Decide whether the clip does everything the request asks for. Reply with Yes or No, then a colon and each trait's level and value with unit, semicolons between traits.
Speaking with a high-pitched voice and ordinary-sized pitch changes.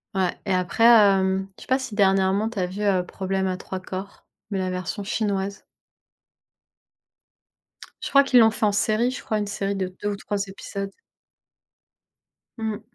No: high, 200 Hz; narrow, 2.1 semitones